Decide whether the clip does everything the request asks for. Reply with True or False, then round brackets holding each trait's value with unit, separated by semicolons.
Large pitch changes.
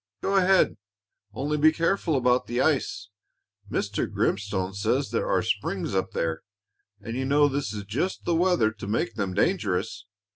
True (7.6 semitones)